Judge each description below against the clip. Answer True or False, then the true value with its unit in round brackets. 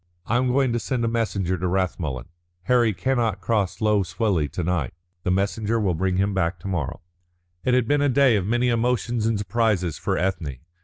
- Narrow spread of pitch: False (4.5 semitones)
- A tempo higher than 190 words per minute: True (200 wpm)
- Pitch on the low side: True (105 Hz)